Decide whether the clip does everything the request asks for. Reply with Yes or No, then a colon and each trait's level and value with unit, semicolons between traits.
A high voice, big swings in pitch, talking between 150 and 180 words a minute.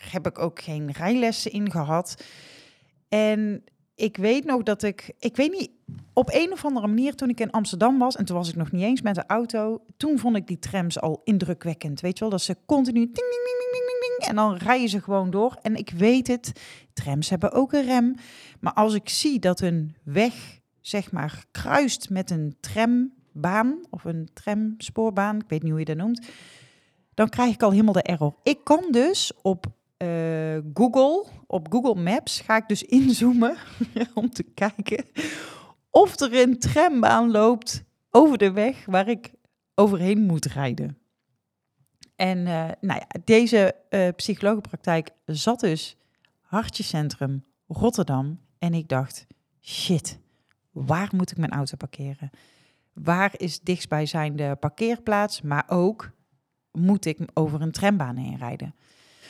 Yes: high, 195 Hz; wide, 6.6 semitones; average, 170 wpm